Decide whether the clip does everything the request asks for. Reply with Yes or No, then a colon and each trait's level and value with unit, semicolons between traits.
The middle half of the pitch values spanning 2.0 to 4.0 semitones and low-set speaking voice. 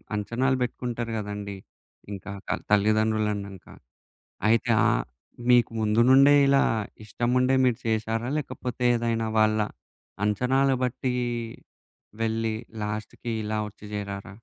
Yes: average, 2.8 semitones; low, 110 Hz